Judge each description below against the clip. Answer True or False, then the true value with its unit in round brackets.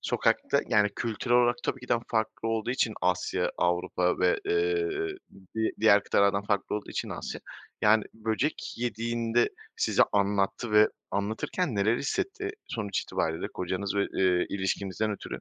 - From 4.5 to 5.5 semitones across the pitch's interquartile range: False (3.0 semitones)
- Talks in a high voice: False (110 Hz)